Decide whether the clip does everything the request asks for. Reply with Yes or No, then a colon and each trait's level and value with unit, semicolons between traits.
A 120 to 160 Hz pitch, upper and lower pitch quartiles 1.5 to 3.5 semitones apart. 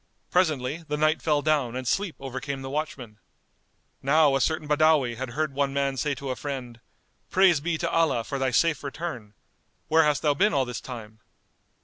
Yes: medium, 140 Hz; average, 3.2 semitones